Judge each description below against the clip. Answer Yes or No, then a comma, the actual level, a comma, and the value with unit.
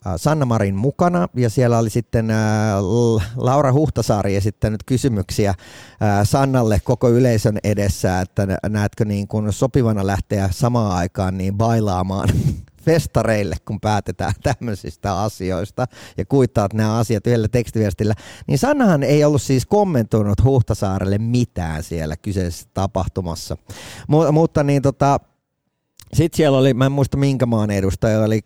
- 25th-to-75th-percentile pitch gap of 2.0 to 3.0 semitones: No, average, 4.4 semitones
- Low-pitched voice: Yes, low, 110 Hz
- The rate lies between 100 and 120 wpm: No, average, 130 wpm